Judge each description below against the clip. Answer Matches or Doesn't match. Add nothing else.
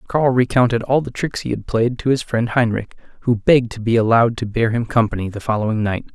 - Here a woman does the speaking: Doesn't match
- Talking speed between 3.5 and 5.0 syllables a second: Doesn't match